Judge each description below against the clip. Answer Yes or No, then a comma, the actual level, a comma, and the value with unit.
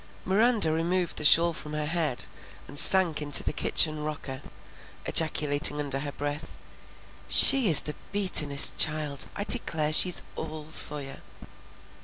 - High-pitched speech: No, medium, 155 Hz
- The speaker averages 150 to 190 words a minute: No, slow, 135 wpm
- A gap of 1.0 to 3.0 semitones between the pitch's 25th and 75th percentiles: Yes, average, 2.7 semitones